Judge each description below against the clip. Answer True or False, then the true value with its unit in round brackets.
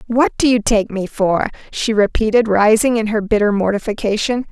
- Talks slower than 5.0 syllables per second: False (5.2 syllables/s)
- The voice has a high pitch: True (215 Hz)